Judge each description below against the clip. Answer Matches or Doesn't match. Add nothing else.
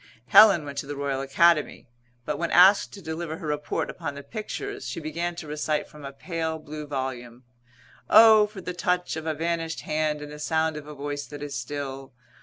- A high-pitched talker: Doesn't match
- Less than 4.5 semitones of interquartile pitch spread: Matches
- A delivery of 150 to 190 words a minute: Doesn't match